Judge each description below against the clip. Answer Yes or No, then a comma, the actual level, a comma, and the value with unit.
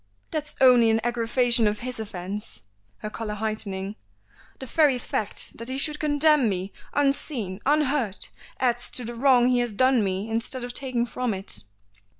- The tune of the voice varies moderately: Yes, average, 3.7 semitones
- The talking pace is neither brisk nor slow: Yes, average, 160 wpm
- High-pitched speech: Yes, high, 240 Hz